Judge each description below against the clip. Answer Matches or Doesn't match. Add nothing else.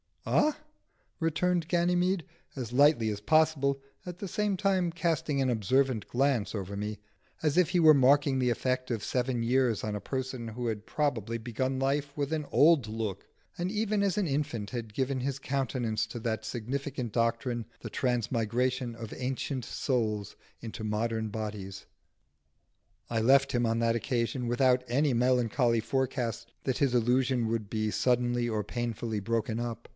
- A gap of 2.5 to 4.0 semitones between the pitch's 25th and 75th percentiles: Matches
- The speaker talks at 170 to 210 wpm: Doesn't match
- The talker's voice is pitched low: Matches